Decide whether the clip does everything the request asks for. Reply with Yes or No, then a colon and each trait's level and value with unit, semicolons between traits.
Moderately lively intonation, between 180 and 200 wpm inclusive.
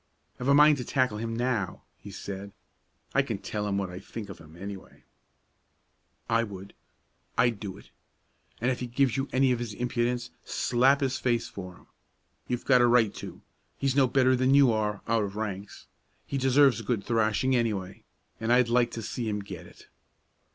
Yes: average, 3.8 semitones; average, 195 wpm